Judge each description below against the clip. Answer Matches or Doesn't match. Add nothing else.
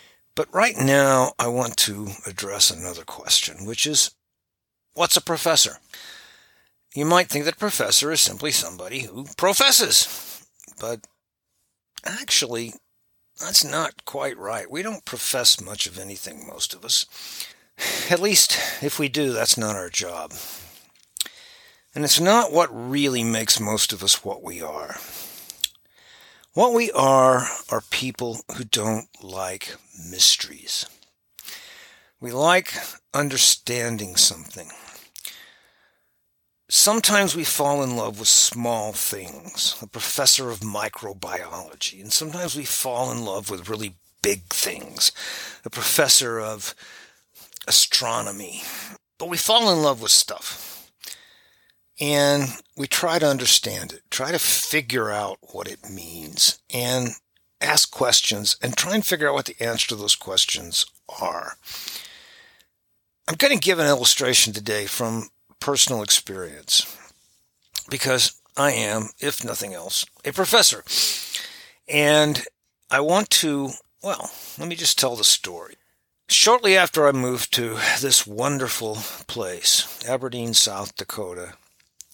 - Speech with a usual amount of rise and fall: Doesn't match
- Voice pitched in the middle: Doesn't match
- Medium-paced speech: Doesn't match